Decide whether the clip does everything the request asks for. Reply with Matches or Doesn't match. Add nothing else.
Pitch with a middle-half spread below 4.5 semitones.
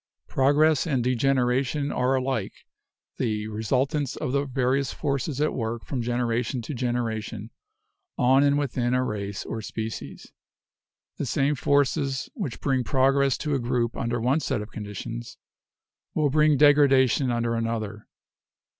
Matches